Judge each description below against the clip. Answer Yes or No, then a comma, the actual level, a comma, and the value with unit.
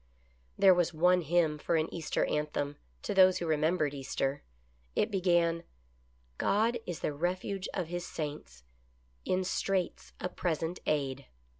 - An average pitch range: Yes, average, 3.6 semitones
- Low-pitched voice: No, medium, 165 Hz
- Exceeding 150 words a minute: No, average, 145 wpm